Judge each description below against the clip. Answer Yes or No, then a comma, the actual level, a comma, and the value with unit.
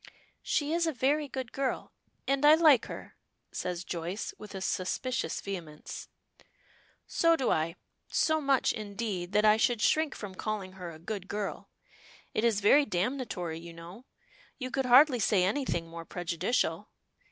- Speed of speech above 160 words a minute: No, average, 155 wpm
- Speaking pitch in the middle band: No, high, 215 Hz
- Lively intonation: Yes, wide, 6.8 semitones